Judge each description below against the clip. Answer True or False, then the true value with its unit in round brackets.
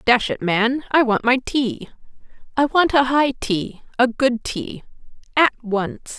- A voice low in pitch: False (245 Hz)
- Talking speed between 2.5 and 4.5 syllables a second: True (3.7 syllables/s)